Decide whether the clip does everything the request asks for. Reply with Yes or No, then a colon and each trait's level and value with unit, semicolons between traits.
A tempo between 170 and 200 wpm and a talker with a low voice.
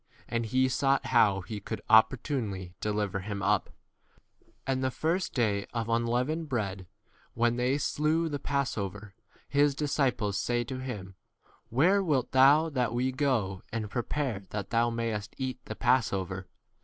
No: average, 160 wpm; low, 120 Hz